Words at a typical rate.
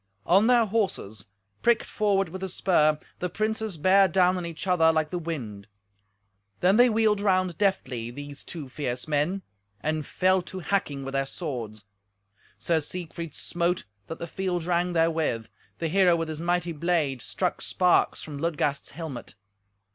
Yes: average, 155 wpm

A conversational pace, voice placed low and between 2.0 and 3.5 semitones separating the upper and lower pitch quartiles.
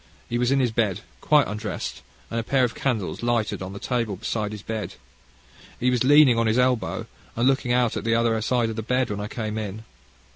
No: fast, 225 wpm; low, 115 Hz; narrow, 2.6 semitones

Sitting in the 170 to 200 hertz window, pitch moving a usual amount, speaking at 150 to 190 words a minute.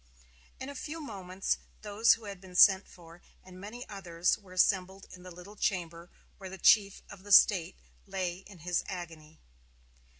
No: high, 190 Hz; narrow, 2.3 semitones; average, 170 wpm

